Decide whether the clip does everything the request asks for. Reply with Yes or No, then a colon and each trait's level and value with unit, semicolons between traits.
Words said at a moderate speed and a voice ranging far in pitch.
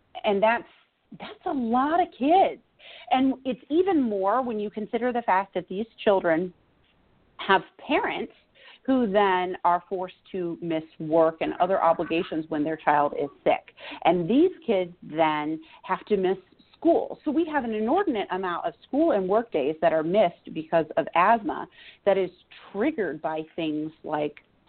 Yes: average, 165 wpm; wide, 7.3 semitones